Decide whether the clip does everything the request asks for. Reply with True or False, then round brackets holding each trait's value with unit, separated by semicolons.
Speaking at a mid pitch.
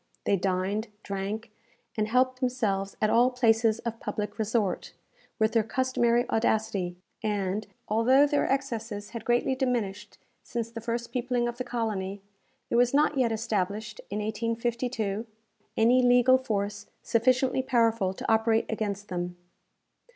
False (225 Hz)